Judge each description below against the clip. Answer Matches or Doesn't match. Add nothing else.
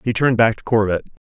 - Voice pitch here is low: Matches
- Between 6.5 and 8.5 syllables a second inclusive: Matches